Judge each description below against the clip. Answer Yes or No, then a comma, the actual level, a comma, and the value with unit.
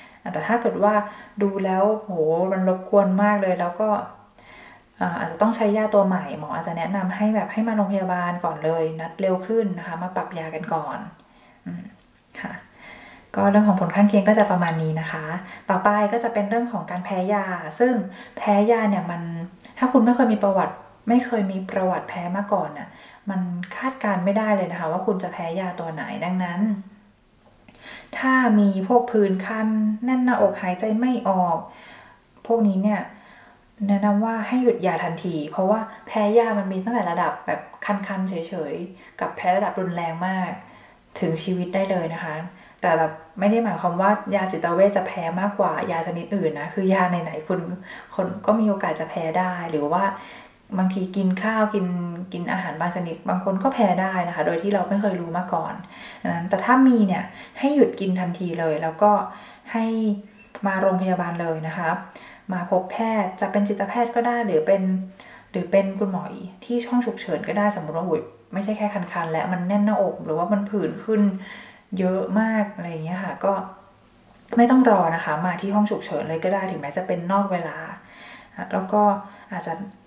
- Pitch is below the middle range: No, high, 195 Hz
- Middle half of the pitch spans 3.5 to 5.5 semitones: No, average, 2.9 semitones